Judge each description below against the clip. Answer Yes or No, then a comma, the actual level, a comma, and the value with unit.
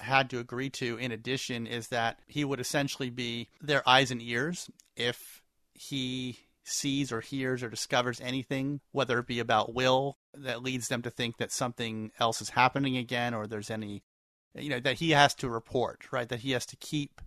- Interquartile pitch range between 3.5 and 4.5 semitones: No, narrow, 2.4 semitones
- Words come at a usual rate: Yes, average, 195 wpm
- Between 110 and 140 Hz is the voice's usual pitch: Yes, low, 125 Hz